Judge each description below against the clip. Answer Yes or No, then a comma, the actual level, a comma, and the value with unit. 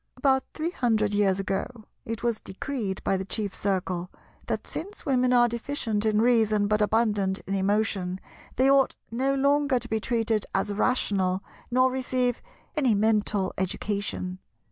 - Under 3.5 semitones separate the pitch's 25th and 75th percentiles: No, average, 4.1 semitones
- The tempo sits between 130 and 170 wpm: Yes, average, 150 wpm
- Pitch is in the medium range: No, high, 220 Hz